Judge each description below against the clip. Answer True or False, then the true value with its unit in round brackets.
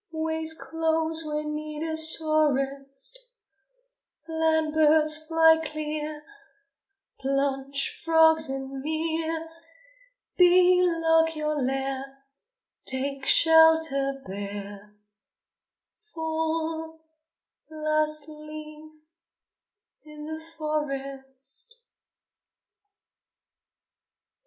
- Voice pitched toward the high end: True (310 Hz)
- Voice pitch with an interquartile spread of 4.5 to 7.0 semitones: False (2.7 semitones)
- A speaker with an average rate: False (65 wpm)